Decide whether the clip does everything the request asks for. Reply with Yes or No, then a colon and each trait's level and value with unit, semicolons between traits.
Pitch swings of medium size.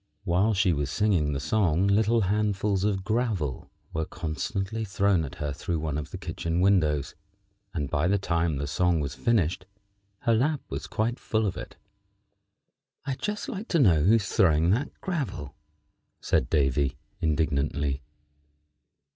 No: wide, 6.0 semitones